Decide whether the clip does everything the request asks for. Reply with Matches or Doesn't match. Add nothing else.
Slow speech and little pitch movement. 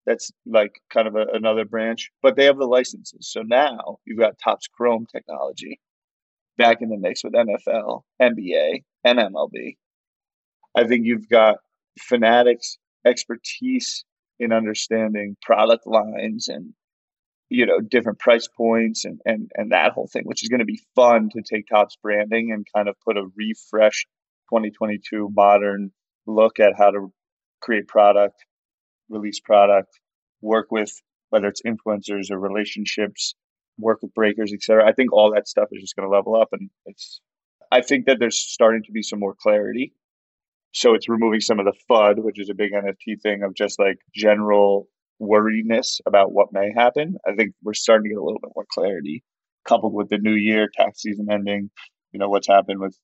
Doesn't match